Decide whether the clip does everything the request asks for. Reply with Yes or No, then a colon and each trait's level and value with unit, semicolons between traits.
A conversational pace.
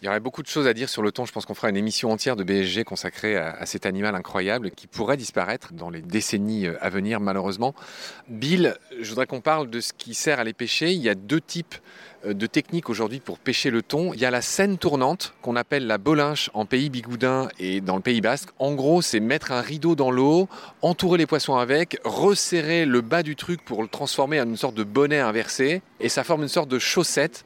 No: fast, 240 wpm